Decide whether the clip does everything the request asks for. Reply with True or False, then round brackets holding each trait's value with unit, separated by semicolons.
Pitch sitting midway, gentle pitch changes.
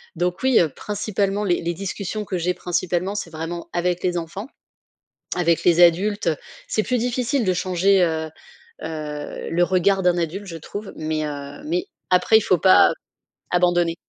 False (180 Hz; 3.1 semitones)